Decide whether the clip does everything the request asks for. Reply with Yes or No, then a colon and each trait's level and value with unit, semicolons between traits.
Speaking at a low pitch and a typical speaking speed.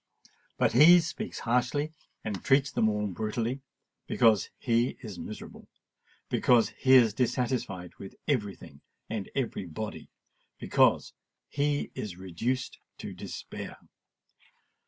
No: low, 115 Hz; slow, 110 wpm